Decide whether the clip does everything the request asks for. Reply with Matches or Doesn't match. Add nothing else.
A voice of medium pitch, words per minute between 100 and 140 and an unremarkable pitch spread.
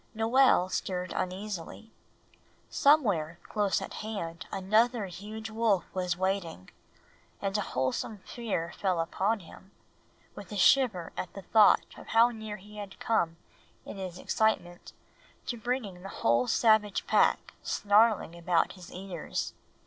Doesn't match